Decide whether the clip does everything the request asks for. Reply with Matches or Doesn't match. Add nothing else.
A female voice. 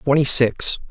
Doesn't match